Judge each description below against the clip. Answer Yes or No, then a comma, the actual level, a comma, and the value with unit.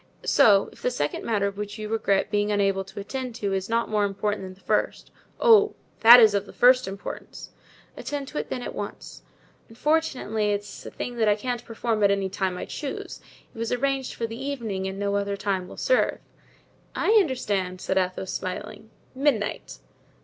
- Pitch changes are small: No, average, 3.8 semitones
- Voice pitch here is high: Yes, high, 210 Hz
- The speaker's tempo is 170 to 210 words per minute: Yes, average, 195 wpm